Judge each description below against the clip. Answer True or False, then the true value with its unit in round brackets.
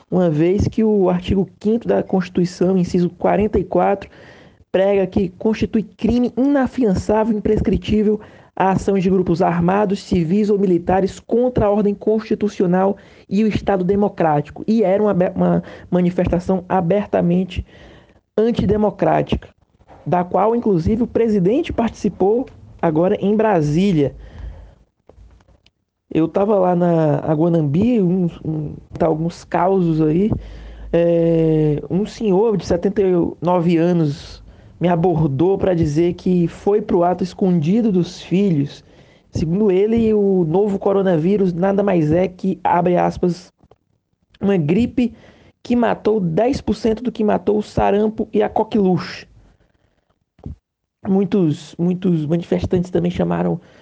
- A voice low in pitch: False (190 Hz)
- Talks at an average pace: False (115 wpm)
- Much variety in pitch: False (3.4 semitones)